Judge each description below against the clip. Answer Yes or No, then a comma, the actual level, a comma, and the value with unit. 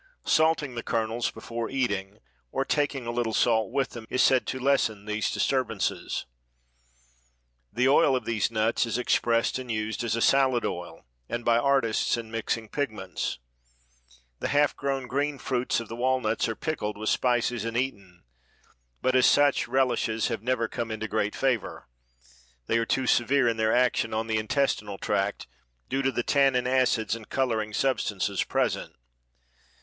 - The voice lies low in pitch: Yes, low, 120 Hz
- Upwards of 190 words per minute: No, average, 165 wpm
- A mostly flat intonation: No, average, 3.0 semitones